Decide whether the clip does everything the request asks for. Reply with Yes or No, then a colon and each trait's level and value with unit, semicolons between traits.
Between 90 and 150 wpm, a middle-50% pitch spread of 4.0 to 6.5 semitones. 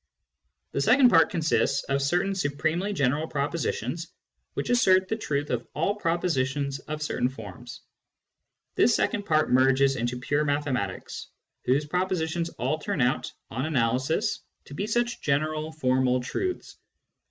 Yes: slow, 135 wpm; average, 4.6 semitones